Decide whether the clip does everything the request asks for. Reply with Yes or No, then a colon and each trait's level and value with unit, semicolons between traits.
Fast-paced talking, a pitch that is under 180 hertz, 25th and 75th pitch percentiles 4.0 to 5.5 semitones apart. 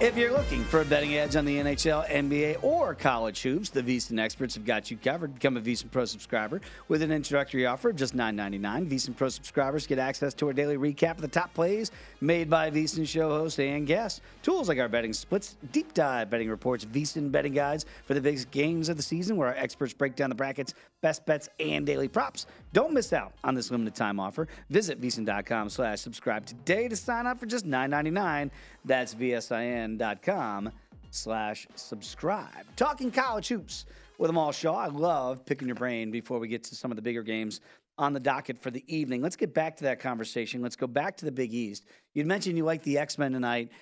Yes: fast, 210 wpm; medium, 140 Hz; average, 4.5 semitones